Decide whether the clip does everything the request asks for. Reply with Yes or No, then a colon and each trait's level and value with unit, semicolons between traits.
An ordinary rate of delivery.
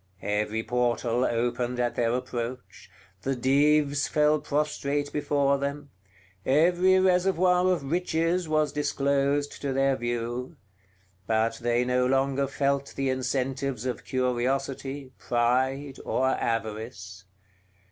No: slow, 110 wpm